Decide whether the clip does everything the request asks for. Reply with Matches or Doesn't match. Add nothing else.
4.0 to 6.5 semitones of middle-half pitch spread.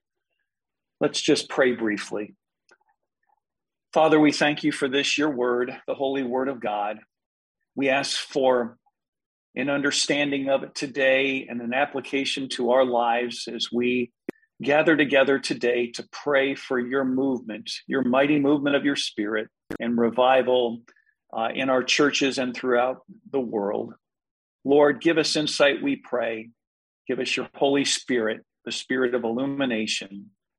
Doesn't match